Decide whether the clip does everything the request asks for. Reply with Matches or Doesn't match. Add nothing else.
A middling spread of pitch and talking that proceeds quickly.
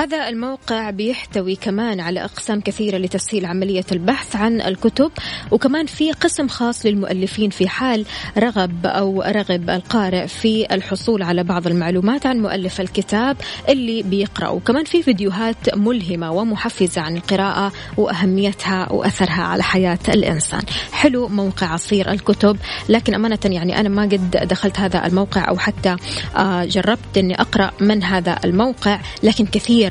Matches